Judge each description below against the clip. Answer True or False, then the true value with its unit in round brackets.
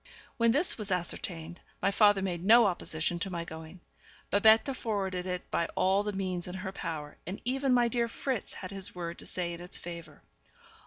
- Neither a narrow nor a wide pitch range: True (3.7 semitones)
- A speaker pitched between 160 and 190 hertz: True (185 Hz)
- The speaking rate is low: False (195 wpm)